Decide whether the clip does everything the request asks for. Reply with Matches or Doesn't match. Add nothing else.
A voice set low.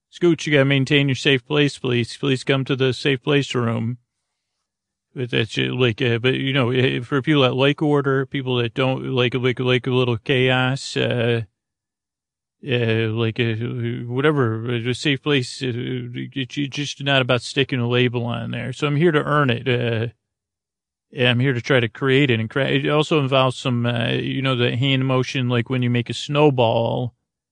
Matches